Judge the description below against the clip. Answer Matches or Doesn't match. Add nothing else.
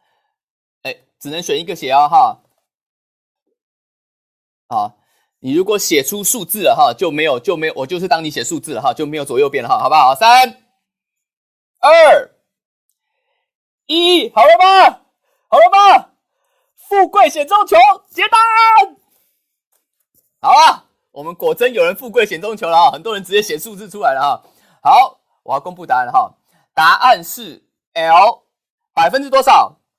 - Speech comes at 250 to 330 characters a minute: Doesn't match